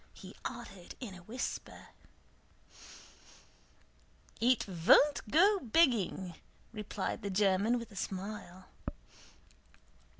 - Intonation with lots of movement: No, average, 4.6 semitones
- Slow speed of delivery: Yes, slow, 90 wpm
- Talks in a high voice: Yes, high, 210 Hz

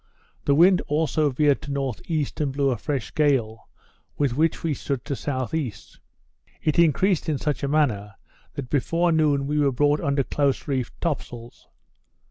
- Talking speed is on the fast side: No, average, 165 wpm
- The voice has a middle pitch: Yes, medium, 145 Hz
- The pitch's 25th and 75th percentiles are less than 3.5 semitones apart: Yes, narrow, 2.6 semitones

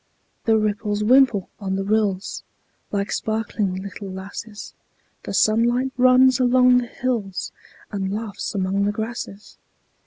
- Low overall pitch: No, high, 215 Hz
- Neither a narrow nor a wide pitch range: Yes, average, 3.3 semitones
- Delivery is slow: Yes, slow, 125 wpm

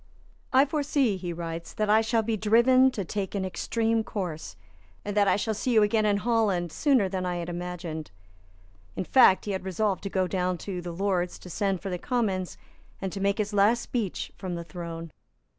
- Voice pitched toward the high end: Yes, high, 195 Hz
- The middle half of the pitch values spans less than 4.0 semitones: Yes, average, 3.6 semitones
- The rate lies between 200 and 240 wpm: Yes, fast, 205 wpm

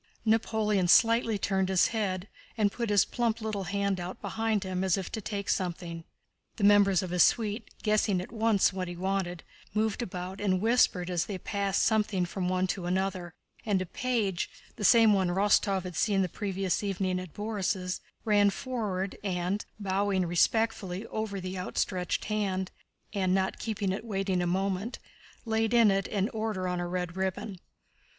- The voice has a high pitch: Yes, high, 195 Hz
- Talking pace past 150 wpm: Yes, average, 170 wpm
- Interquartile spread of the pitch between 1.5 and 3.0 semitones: Yes, narrow, 2.5 semitones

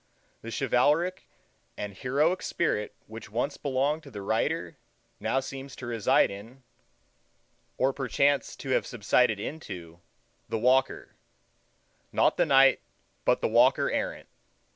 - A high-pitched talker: No, low, 130 Hz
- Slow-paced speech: Yes, slow, 120 wpm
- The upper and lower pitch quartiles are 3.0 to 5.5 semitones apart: Yes, average, 3.9 semitones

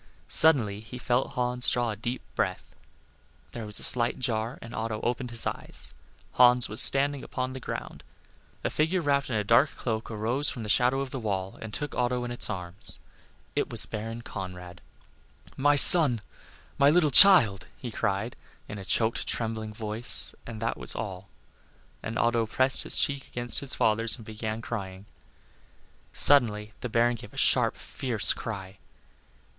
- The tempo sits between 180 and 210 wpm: No, average, 170 wpm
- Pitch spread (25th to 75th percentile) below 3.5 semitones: Yes, average, 3.0 semitones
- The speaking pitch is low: Yes, low, 115 Hz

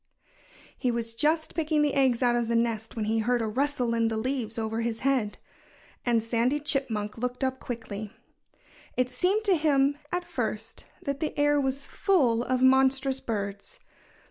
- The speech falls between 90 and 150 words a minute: No, average, 170 wpm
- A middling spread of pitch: Yes, average, 3.7 semitones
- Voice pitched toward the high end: Yes, very high, 250 Hz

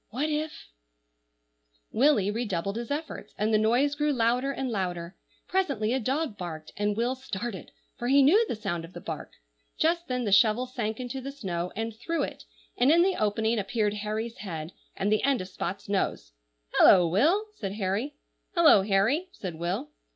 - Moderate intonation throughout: No, wide, 5.7 semitones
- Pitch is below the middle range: No, high, 225 Hz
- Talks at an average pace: Yes, average, 180 wpm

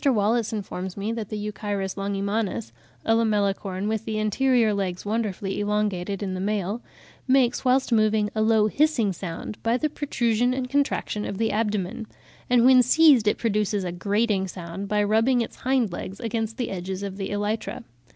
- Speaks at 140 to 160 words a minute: No, average, 170 wpm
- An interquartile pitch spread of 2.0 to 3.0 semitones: Yes, average, 2.7 semitones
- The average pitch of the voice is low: No, high, 210 Hz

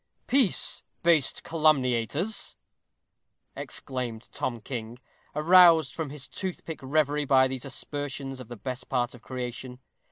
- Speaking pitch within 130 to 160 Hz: Yes, low, 135 Hz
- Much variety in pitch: No, average, 3.9 semitones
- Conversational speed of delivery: No, slow, 125 wpm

